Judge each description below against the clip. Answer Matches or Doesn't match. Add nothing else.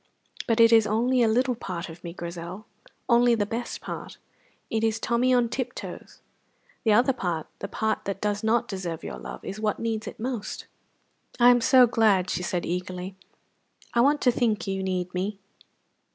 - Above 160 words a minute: Matches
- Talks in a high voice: Matches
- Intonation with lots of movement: Doesn't match